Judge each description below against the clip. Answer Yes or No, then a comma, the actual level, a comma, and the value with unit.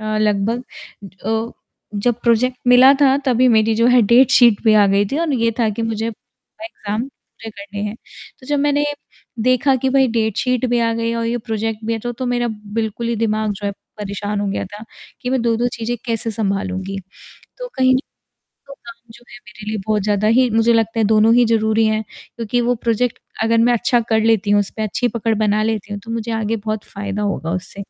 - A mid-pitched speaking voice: No, high, 225 Hz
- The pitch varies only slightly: Yes, narrow, 2.2 semitones